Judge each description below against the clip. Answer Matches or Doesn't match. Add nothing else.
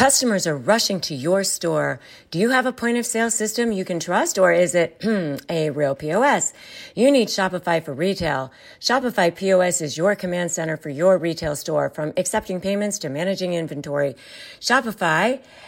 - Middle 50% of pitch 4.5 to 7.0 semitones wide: Matches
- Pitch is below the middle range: Doesn't match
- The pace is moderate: Matches